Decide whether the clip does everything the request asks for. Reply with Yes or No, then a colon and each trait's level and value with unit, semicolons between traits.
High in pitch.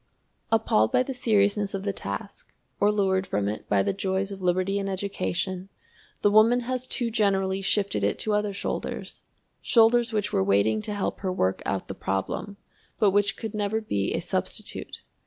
Yes: high, 200 Hz